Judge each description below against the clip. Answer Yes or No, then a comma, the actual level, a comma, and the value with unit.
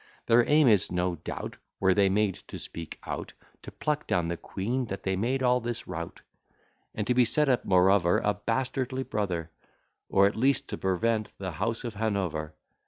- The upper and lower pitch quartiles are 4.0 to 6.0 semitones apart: Yes, average, 4.9 semitones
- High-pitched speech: No, low, 105 Hz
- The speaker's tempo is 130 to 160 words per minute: No, average, 180 wpm